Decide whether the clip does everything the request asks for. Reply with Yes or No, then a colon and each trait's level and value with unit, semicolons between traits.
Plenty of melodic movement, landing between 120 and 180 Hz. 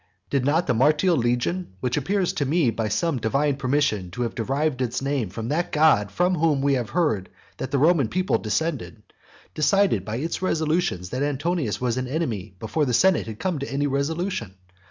Yes: wide, 5.7 semitones; medium, 140 Hz